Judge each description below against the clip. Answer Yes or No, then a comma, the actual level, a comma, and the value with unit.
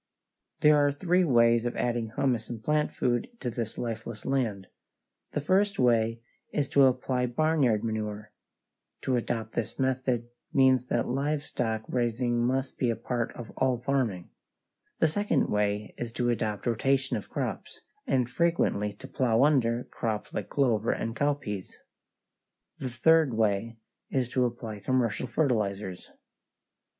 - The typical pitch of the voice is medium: No, low, 120 Hz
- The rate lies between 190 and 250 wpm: No, average, 140 wpm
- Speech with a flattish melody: No, average, 3.1 semitones